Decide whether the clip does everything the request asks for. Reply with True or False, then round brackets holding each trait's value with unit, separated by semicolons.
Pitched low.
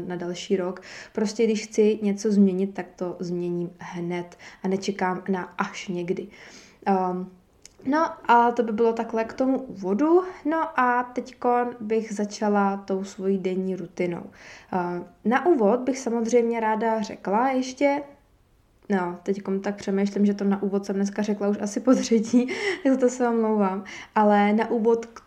False (210 Hz)